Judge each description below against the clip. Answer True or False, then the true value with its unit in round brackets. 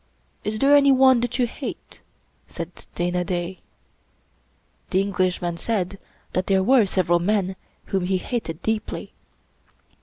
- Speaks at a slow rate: True (125 wpm)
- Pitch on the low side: False (190 Hz)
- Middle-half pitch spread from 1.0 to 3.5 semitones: False (4.3 semitones)